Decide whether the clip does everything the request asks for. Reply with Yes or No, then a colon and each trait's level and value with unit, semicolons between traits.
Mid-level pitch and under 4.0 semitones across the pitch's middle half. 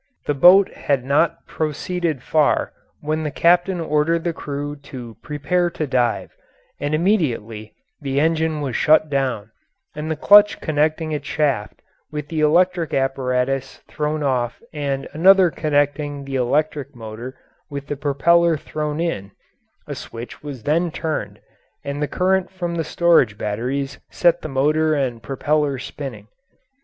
Yes: medium, 150 Hz; average, 3.2 semitones